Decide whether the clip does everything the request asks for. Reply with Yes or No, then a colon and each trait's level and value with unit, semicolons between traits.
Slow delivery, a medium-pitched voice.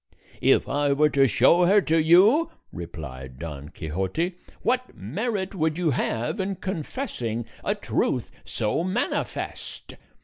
Yes: slow, 130 wpm; medium, 155 Hz